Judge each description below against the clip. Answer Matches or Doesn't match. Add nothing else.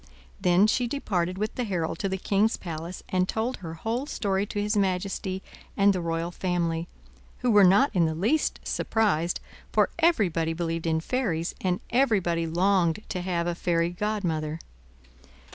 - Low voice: Doesn't match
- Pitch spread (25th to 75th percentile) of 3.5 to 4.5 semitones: Matches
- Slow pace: Doesn't match